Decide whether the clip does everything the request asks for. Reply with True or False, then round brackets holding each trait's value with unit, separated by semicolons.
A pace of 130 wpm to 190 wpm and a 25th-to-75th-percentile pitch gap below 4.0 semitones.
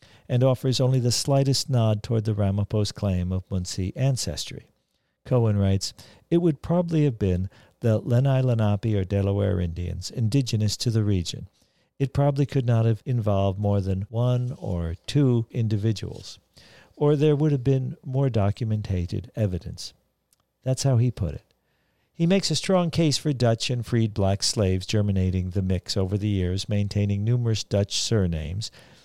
False (155 wpm; 4.7 semitones)